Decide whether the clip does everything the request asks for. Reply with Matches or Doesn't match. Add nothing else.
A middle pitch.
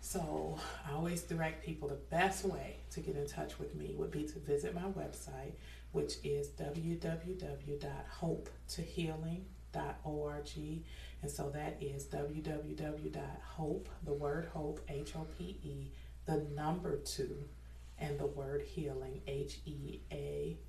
Matches